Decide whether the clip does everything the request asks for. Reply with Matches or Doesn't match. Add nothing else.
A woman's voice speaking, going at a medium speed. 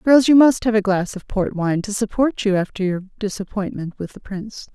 Doesn't match